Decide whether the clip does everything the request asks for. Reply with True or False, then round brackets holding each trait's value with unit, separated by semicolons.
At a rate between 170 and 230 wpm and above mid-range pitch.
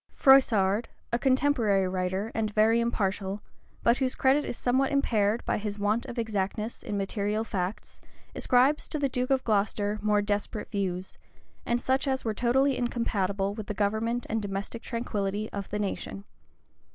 False (160 wpm; 215 Hz)